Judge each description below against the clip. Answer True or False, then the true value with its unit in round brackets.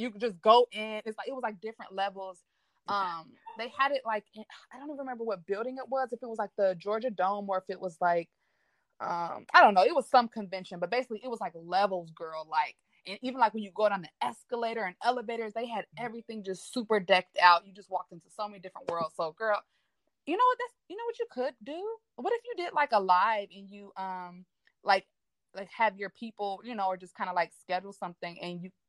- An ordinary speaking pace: False (245 wpm)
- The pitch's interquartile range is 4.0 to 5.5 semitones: True (4.6 semitones)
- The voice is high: True (210 Hz)